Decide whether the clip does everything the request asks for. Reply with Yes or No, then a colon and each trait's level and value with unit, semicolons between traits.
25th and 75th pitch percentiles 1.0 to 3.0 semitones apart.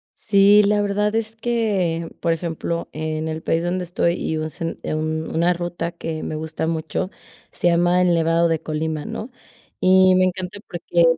Yes: average, 2.7 semitones